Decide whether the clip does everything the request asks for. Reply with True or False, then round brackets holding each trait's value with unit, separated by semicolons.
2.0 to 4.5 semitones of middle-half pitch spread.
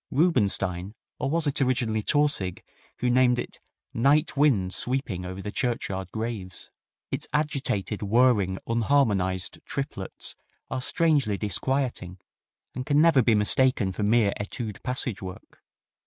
False (5.5 semitones)